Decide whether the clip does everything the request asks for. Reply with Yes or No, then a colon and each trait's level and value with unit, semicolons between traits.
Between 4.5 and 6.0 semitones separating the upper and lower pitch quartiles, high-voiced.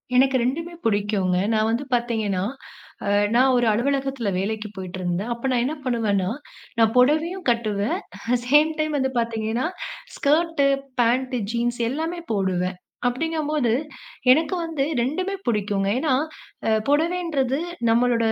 Yes: wide, 5.4 semitones; high, 245 Hz